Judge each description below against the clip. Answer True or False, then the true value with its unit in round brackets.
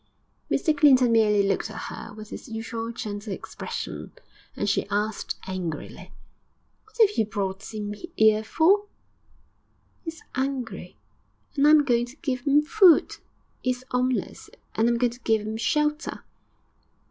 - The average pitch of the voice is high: True (235 Hz)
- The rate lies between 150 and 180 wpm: True (155 wpm)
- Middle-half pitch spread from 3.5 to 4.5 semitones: False (5.0 semitones)